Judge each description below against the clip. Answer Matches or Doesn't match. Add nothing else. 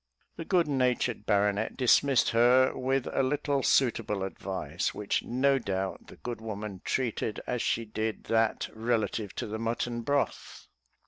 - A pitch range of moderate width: Matches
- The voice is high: Doesn't match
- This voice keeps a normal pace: Matches